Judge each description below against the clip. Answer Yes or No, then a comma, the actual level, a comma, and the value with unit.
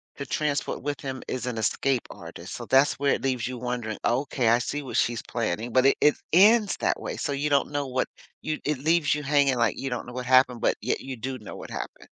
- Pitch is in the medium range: No, low, 130 Hz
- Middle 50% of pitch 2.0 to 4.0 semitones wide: Yes, average, 2.8 semitones